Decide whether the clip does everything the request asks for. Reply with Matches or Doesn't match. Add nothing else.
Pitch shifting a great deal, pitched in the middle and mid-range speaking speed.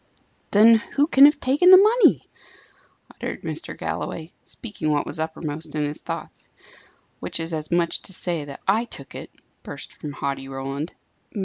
Matches